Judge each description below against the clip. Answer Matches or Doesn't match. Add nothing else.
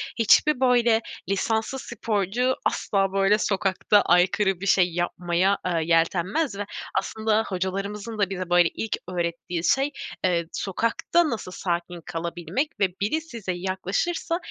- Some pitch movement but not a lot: Matches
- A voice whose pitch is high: Matches